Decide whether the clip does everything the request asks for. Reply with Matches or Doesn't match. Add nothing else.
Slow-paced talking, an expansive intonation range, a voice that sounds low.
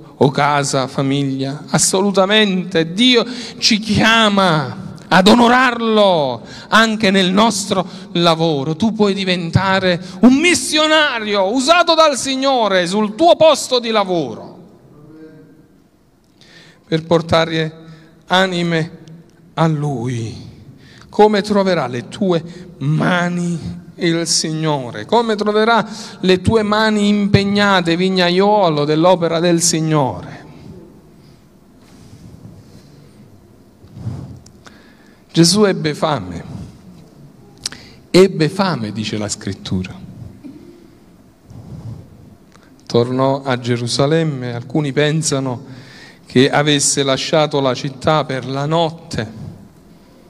Doesn't match